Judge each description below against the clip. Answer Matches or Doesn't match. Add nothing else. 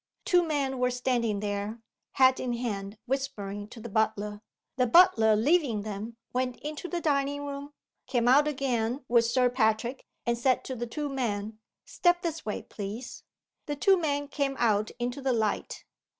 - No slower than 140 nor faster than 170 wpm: Matches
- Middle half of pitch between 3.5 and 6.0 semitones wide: Matches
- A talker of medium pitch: Doesn't match